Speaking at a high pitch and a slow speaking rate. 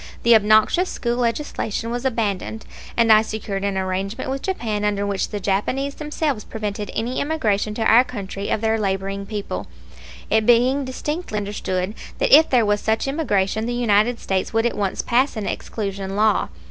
No: high, 220 Hz; average, 170 wpm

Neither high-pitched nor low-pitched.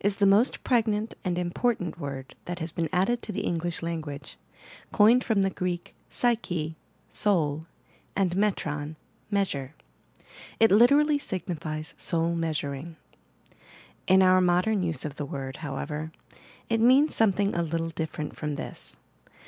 Yes: medium, 175 Hz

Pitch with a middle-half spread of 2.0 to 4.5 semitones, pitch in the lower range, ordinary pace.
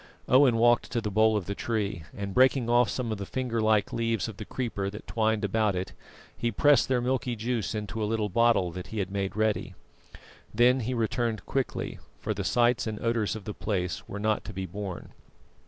No: average, 2.8 semitones; low, 110 Hz; fast, 210 wpm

